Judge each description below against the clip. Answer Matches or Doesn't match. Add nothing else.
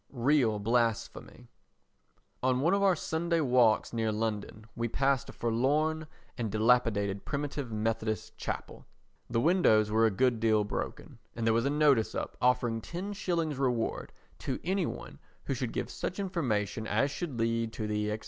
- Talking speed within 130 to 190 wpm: Matches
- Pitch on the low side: Matches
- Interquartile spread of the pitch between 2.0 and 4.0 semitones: Doesn't match